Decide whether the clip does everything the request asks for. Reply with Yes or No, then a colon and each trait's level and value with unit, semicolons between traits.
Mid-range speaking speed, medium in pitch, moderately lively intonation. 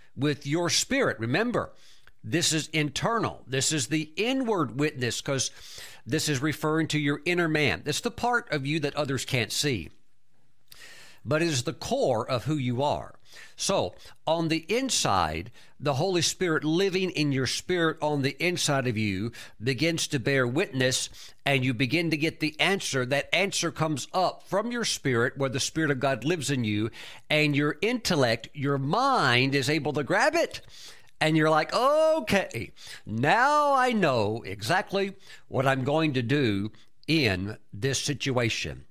Yes: average, 160 wpm; medium, 150 Hz; average, 3.6 semitones